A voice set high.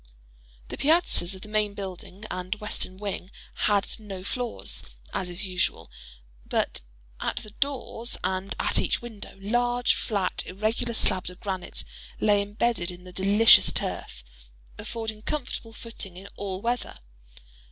Yes: high, 205 Hz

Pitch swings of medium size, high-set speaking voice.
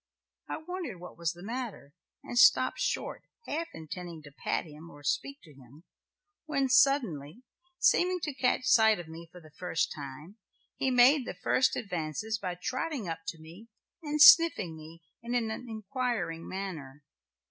No: wide, 8.0 semitones; high, 195 Hz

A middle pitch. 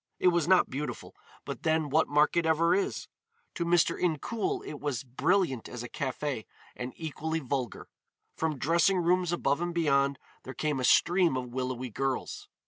Yes: medium, 155 Hz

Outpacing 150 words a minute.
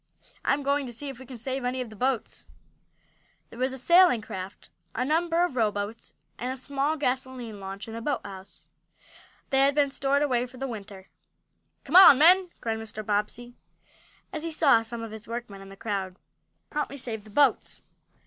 Yes: average, 190 wpm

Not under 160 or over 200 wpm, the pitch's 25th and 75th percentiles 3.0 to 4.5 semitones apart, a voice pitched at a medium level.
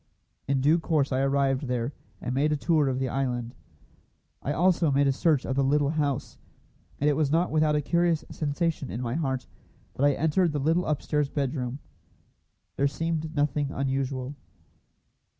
No: average, 170 wpm; narrow, 2.4 semitones; medium, 145 Hz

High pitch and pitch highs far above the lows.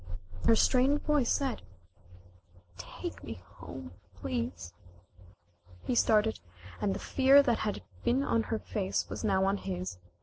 Yes: high, 215 Hz; wide, 5.7 semitones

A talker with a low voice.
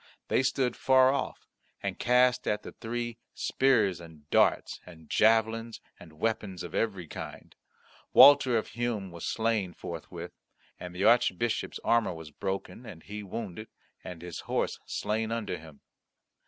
Yes: low, 110 Hz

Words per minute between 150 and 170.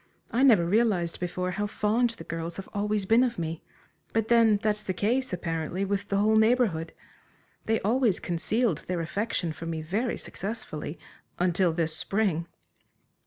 Yes: average, 160 wpm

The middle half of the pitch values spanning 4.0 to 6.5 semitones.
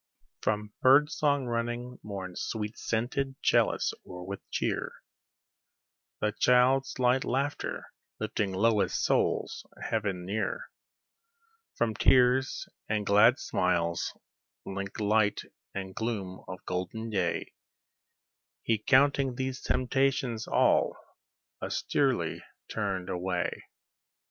Yes: average, 4.7 semitones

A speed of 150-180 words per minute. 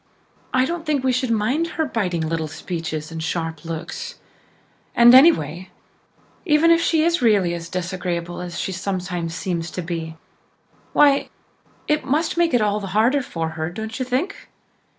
Yes: average, 165 wpm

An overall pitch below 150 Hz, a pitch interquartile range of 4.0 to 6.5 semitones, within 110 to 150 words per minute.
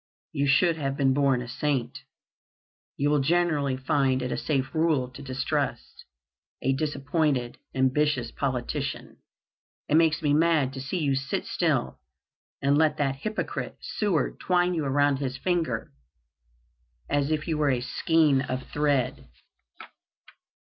No: medium, 140 Hz; average, 2.8 semitones; average, 140 wpm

